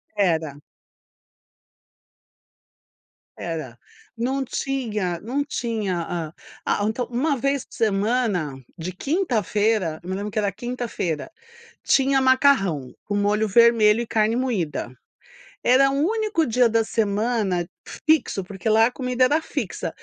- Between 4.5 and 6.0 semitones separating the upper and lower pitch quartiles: Yes, average, 5.0 semitones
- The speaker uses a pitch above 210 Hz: Yes, high, 220 Hz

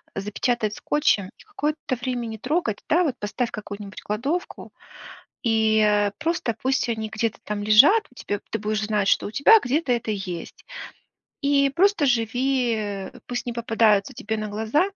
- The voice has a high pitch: Yes, high, 230 Hz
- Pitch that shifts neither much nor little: Yes, average, 4.6 semitones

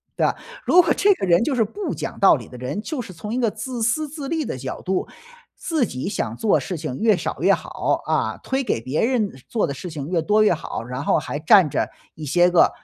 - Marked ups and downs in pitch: Yes, wide, 8.3 semitones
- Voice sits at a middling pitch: No, high, 200 Hz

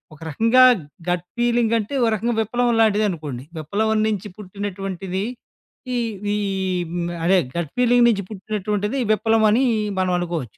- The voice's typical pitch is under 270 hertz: Yes, high, 210 Hz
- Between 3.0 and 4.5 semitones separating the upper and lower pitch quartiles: Yes, average, 3.8 semitones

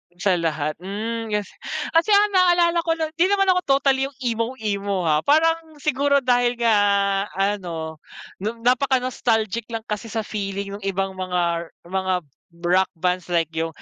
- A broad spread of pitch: Yes, wide, 6.0 semitones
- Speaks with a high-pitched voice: Yes, high, 215 Hz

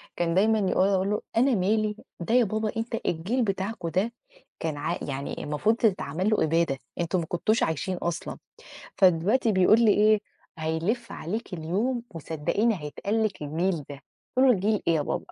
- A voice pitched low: No, high, 190 Hz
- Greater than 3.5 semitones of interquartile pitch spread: Yes, average, 4.9 semitones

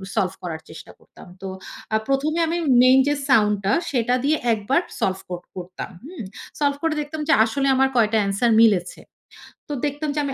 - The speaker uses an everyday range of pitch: No, wide, 6.6 semitones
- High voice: Yes, very high, 250 Hz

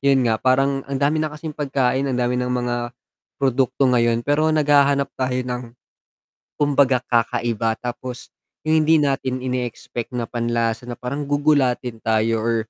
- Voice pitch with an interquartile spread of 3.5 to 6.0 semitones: No, average, 2.7 semitones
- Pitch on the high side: No, low, 125 Hz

